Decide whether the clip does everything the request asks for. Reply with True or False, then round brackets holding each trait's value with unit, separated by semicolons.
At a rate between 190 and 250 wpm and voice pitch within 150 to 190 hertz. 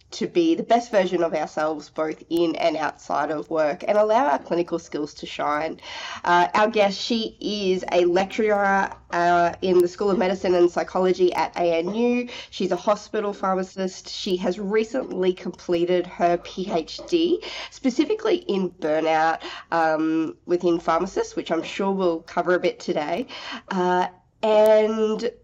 False (150 wpm; 185 Hz)